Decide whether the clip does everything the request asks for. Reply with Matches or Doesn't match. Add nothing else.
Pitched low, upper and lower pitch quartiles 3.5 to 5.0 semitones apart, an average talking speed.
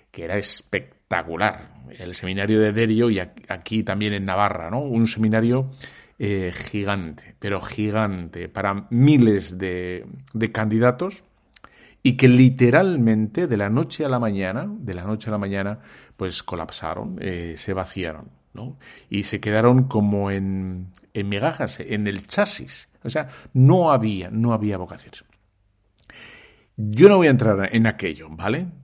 Matches